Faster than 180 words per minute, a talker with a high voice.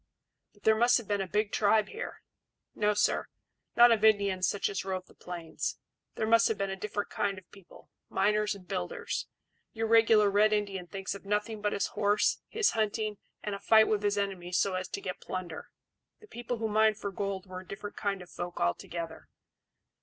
Yes: average, 200 wpm; high, 205 Hz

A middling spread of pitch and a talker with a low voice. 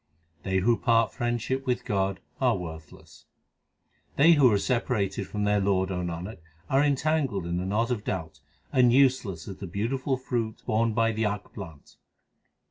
Yes: average, 4.6 semitones; low, 110 Hz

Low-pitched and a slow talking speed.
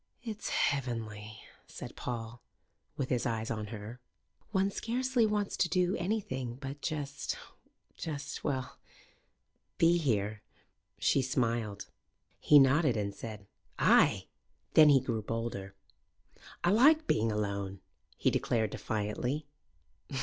Yes: low, 125 Hz; slow, 115 wpm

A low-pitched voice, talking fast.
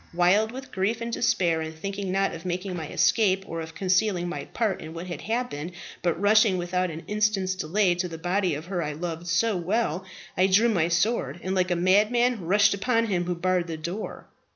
No: medium, 185 Hz; fast, 210 wpm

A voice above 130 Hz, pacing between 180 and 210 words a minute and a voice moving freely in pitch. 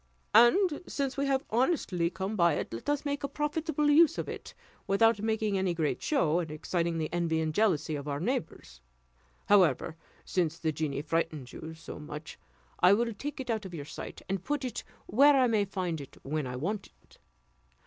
Yes: high, 190 Hz; average, 195 wpm; wide, 8.3 semitones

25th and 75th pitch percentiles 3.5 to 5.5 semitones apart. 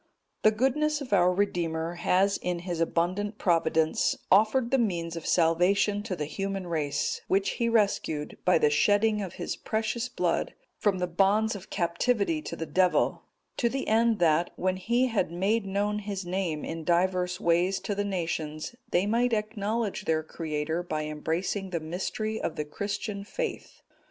Yes: average, 4.1 semitones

